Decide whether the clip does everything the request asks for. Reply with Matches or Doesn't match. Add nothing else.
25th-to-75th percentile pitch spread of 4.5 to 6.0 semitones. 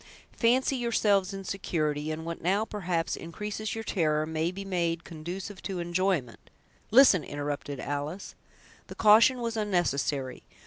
Matches